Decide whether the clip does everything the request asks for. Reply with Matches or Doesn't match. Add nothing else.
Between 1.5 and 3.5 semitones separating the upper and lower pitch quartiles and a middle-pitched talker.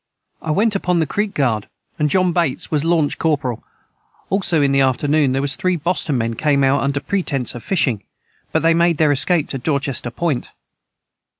Doesn't match